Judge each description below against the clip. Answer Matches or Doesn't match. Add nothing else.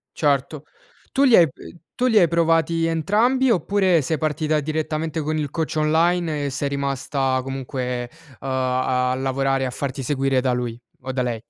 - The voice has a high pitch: Doesn't match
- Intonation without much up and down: Doesn't match